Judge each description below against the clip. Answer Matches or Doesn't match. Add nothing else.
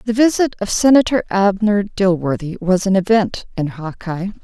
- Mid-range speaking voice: Doesn't match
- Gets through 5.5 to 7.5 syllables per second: Doesn't match